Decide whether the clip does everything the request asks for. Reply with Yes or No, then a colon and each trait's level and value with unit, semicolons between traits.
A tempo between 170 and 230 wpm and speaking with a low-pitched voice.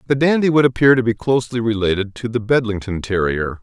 Yes: average, 200 wpm; low, 115 Hz